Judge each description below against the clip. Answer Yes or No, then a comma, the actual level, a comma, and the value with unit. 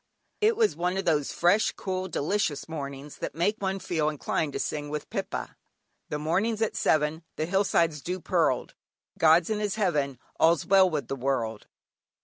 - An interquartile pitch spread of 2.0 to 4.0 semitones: No, average, 4.5 semitones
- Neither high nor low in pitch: Yes, medium, 165 Hz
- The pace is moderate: Yes, average, 170 wpm